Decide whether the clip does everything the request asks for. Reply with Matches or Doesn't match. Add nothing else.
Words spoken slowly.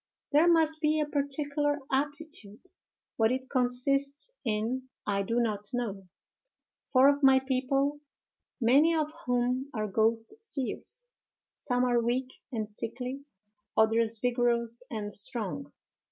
Matches